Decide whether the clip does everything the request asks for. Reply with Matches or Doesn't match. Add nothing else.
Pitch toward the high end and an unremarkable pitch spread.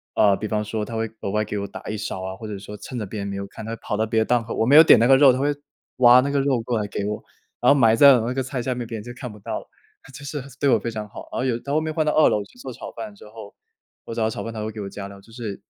Doesn't match